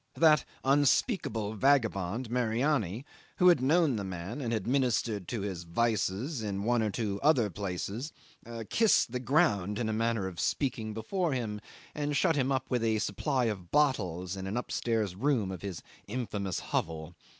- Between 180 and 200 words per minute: No, average, 165 wpm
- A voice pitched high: No, low, 115 Hz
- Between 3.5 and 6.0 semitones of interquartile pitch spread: Yes, average, 5.2 semitones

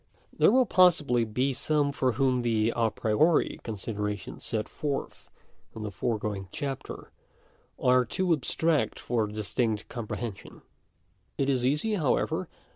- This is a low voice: Yes, low, 125 Hz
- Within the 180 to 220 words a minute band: No, average, 140 wpm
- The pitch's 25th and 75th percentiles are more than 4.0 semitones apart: Yes, average, 4.9 semitones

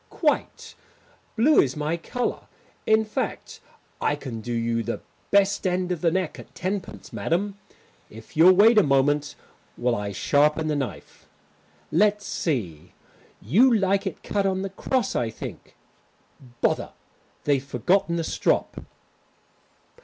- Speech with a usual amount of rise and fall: No, wide, 6.6 semitones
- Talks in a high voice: No, medium, 170 Hz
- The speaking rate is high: No, average, 140 wpm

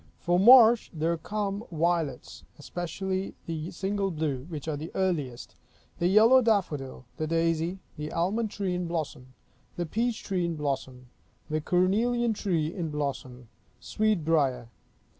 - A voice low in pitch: No, medium, 170 Hz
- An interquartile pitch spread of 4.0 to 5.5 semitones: Yes, average, 4.6 semitones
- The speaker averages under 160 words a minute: Yes, average, 140 wpm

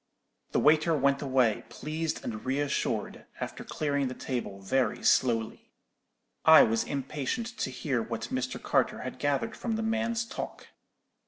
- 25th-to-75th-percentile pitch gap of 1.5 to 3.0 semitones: No, average, 4.0 semitones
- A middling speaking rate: Yes, average, 150 wpm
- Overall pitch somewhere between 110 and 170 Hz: Yes, medium, 140 Hz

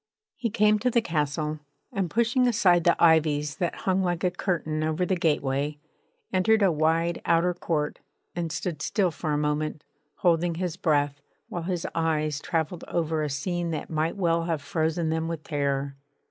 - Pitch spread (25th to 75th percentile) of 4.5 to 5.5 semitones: No, average, 2.7 semitones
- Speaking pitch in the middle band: Yes, medium, 165 Hz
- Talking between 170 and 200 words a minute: Yes, average, 175 wpm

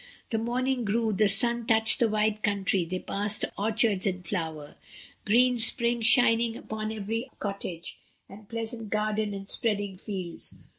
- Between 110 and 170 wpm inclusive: Yes, average, 145 wpm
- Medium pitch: No, high, 215 Hz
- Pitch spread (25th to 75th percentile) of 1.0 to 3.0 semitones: Yes, narrow, 2.5 semitones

